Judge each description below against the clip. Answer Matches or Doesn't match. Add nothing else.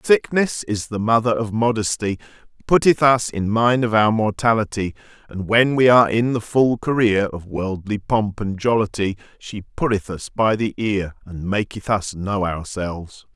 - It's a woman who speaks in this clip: Doesn't match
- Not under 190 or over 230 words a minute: Doesn't match